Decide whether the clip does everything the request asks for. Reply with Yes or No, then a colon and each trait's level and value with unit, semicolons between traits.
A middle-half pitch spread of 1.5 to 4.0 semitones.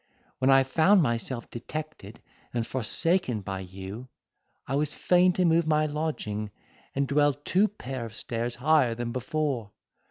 No: average, 4.9 semitones